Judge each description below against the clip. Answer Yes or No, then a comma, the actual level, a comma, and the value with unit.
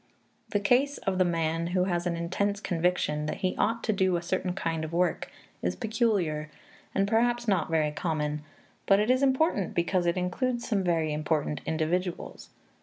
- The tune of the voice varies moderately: Yes, average, 3.9 semitones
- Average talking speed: Yes, average, 180 wpm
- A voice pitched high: No, medium, 180 Hz